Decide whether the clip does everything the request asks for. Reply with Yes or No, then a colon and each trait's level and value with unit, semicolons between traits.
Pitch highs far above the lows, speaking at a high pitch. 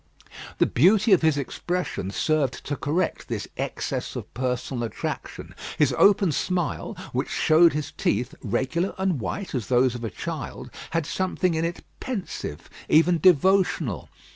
No: wide, 6.2 semitones; medium, 155 Hz